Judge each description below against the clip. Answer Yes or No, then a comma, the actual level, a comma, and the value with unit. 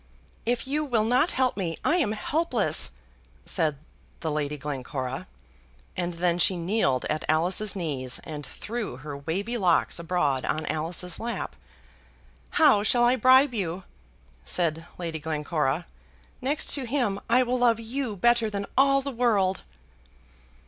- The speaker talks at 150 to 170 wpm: No, average, 140 wpm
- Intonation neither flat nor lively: No, wide, 7.3 semitones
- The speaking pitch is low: No, high, 195 Hz